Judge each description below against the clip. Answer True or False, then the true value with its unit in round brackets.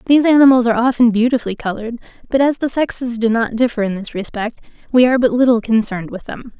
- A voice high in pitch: True (235 Hz)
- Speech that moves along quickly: True (210 wpm)